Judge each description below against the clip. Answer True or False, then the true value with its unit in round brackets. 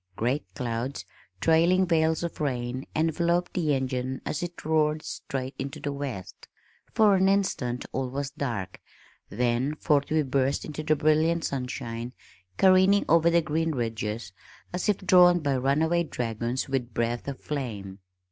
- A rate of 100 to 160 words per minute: True (145 wpm)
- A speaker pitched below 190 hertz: True (140 Hz)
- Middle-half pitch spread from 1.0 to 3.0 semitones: False (4.6 semitones)